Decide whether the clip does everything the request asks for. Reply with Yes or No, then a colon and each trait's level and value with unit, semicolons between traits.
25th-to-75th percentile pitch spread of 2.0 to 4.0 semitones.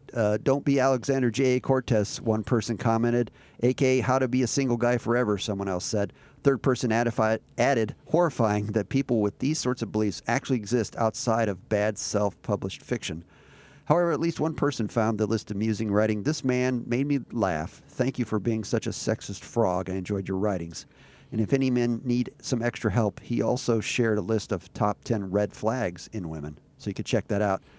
Yes: average, 3.4 semitones